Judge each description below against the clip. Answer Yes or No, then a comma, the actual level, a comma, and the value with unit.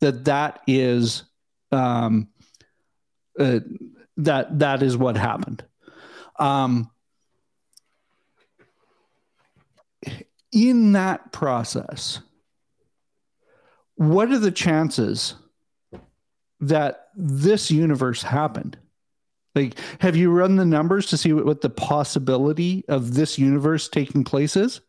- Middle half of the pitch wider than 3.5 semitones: Yes, wide, 5.5 semitones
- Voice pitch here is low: No, medium, 150 Hz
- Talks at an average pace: No, slow, 95 wpm